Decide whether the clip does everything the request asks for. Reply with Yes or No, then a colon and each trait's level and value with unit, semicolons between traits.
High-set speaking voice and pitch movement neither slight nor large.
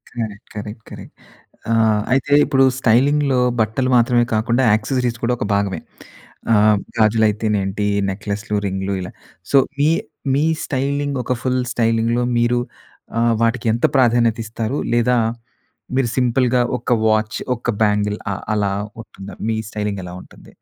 No: low, 115 Hz; average, 3.0 semitones